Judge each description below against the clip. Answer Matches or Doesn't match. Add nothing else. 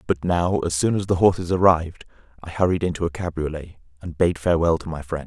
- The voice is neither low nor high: Doesn't match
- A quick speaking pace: Matches